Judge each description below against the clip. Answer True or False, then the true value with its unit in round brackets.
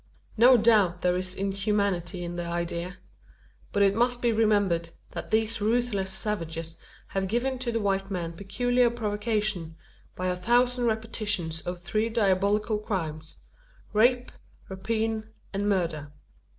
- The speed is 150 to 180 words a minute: False (135 wpm)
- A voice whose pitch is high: True (200 Hz)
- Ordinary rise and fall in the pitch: True (3.8 semitones)